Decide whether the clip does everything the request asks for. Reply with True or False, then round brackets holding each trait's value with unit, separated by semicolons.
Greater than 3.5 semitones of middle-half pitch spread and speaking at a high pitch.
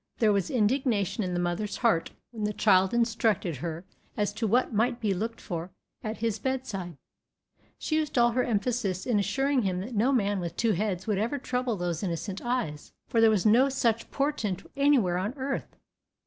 True (4.5 semitones; 215 Hz)